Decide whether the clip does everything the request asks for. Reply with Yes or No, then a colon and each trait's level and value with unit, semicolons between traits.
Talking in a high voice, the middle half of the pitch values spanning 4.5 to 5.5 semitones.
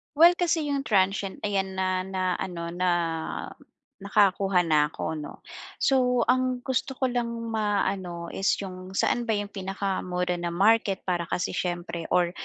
No: high, 195 Hz; average, 4.0 semitones